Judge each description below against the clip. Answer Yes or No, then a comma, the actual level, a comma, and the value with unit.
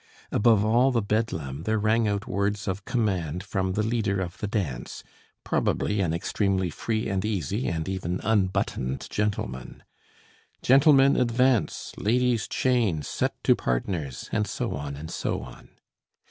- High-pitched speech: No, low, 100 Hz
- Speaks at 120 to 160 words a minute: Yes, average, 145 wpm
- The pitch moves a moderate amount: Yes, average, 4.6 semitones